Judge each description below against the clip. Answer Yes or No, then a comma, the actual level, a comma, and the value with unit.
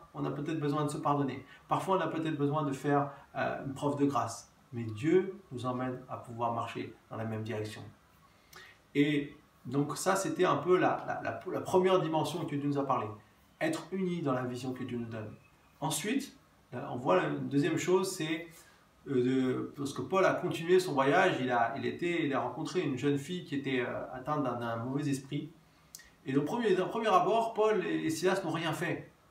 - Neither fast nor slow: Yes, average, 200 wpm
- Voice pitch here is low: No, medium, 145 Hz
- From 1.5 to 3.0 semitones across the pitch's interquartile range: No, average, 4.7 semitones